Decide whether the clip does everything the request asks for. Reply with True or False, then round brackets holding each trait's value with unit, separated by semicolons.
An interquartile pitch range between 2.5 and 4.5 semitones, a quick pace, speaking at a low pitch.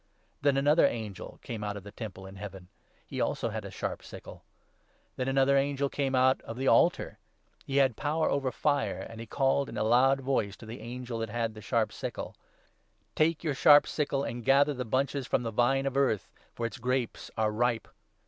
True (3.5 semitones; 215 wpm; 125 Hz)